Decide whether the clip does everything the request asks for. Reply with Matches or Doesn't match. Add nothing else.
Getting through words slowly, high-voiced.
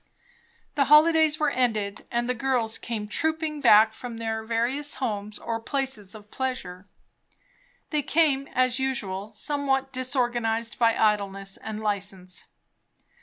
Matches